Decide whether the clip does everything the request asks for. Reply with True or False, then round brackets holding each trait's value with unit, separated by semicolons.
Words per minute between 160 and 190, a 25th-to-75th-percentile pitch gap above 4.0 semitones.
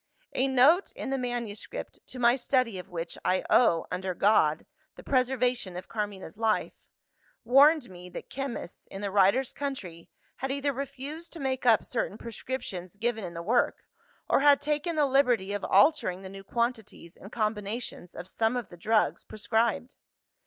True (165 wpm; 5.3 semitones)